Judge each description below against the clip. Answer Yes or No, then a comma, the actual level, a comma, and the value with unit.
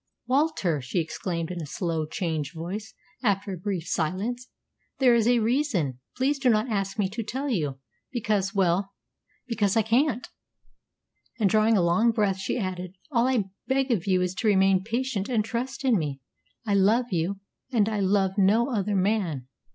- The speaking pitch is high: Yes, high, 205 Hz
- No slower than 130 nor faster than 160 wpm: No, average, 175 wpm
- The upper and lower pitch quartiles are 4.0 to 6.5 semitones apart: Yes, average, 4.4 semitones